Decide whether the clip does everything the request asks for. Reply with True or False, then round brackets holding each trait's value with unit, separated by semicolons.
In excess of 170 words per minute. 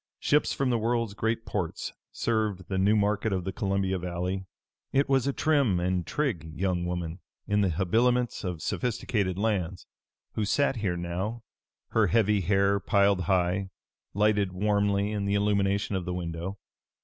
False (160 wpm)